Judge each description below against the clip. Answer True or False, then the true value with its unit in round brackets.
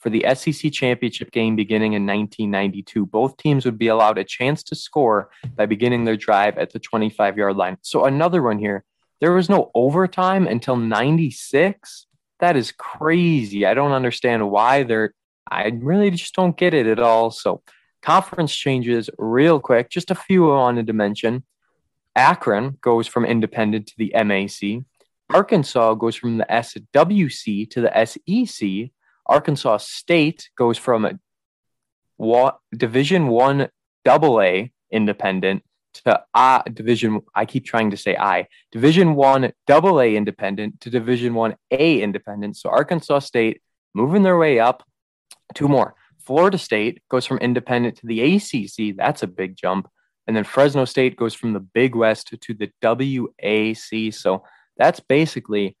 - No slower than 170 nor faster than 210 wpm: False (155 wpm)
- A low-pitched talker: True (120 Hz)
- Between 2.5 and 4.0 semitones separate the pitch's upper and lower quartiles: False (4.5 semitones)